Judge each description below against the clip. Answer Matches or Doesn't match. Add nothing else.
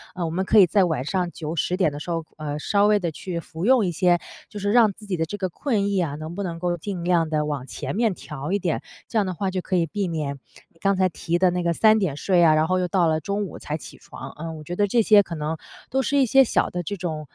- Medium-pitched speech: Matches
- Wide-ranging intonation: Doesn't match